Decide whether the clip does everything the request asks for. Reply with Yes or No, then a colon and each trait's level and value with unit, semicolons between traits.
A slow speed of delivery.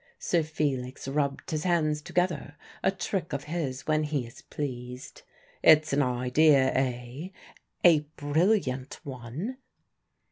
Yes: slow, 120 wpm